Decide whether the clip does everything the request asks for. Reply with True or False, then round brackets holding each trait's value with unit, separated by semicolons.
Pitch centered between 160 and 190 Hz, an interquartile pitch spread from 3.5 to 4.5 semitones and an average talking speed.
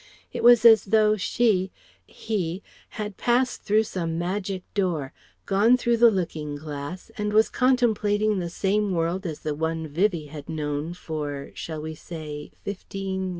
False (185 Hz; 4.9 semitones; 150 wpm)